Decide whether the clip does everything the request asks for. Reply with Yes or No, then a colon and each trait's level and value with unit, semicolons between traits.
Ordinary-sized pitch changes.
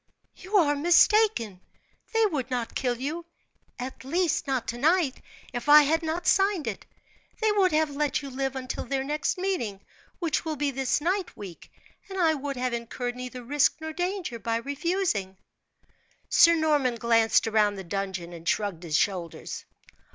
No: wide, 6.2 semitones